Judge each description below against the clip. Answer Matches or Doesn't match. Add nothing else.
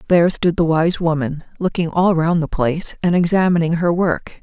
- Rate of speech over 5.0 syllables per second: Matches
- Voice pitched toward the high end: Doesn't match